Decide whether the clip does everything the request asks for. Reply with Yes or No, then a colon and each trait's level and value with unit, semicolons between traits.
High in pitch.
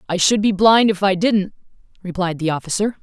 Yes: high, 195 Hz